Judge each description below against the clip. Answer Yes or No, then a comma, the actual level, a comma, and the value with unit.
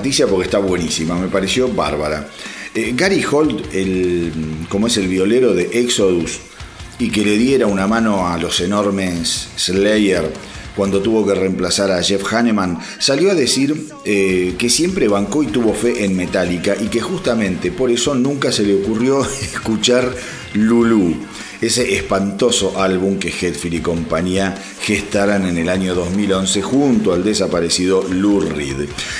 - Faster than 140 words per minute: Yes, average, 150 wpm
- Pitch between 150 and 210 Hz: No, low, 100 Hz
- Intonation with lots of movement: No, average, 3.7 semitones